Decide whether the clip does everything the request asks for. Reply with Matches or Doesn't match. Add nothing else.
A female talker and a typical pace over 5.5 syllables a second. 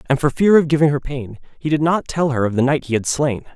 Doesn't match